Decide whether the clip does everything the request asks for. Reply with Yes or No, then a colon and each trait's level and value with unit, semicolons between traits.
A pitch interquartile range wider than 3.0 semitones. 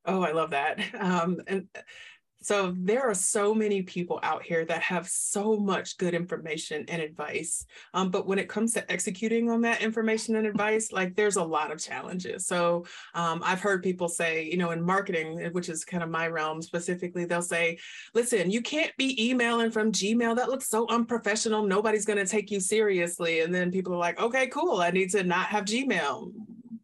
Yes: average, 4.0 semitones